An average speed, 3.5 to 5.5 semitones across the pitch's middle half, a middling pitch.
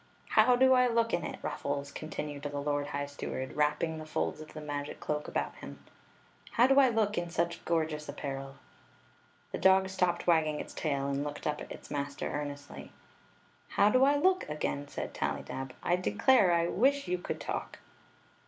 Yes: average, 190 wpm; average, 5.0 semitones; medium, 155 Hz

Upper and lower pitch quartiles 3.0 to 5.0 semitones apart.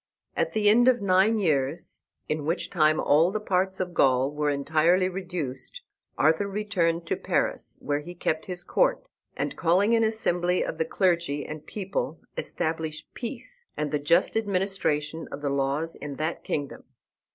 Yes: average, 4.2 semitones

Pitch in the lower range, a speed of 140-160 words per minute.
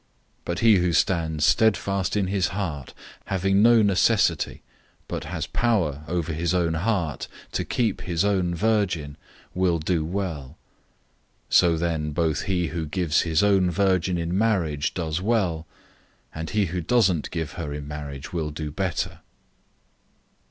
Yes: very low, 85 Hz; average, 145 wpm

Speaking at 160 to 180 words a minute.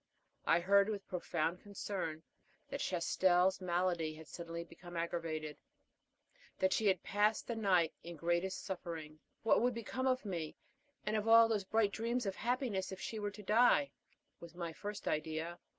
Yes: average, 165 wpm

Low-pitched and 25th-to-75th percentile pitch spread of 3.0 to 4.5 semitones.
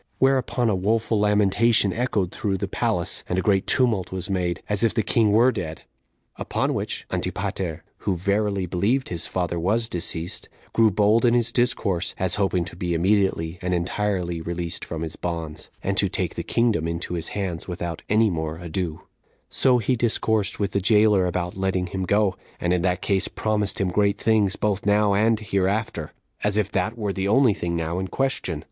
Yes: low, 100 Hz; average, 3.6 semitones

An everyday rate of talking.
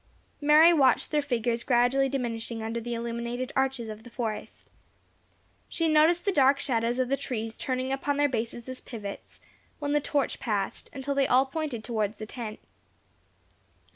Yes: average, 165 wpm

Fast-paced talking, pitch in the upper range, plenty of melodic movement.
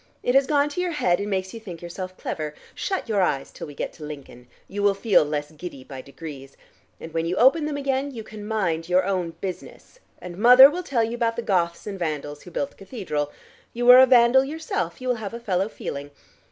Yes: fast, 235 wpm; high, 195 Hz; wide, 7.0 semitones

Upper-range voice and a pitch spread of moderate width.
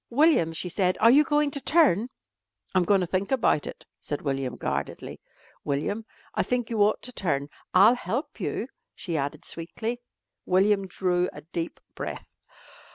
No: high, 195 Hz; wide, 6.3 semitones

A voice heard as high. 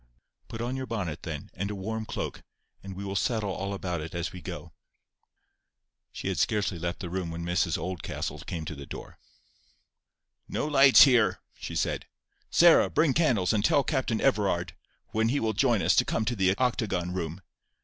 No: low, 100 Hz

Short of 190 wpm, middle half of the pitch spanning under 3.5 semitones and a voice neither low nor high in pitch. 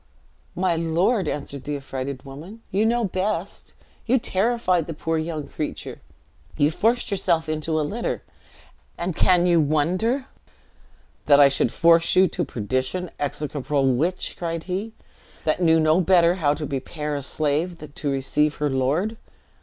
No: average, 155 wpm; average, 4.1 semitones; medium, 165 Hz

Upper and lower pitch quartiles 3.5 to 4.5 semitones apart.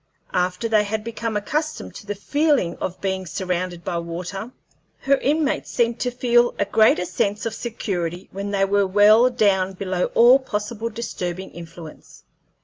Yes: average, 4.2 semitones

